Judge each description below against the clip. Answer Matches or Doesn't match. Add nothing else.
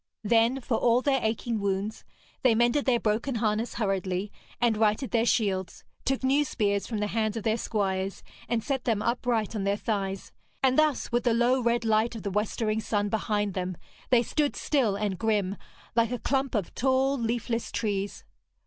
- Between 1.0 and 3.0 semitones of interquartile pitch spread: Matches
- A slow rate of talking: Doesn't match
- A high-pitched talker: Matches